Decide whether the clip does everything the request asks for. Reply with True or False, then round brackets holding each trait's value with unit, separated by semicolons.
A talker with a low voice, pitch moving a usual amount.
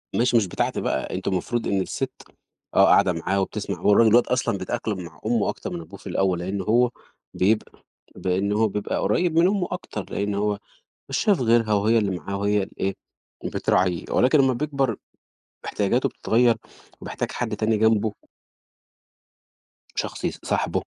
True (105 Hz; 3.5 semitones)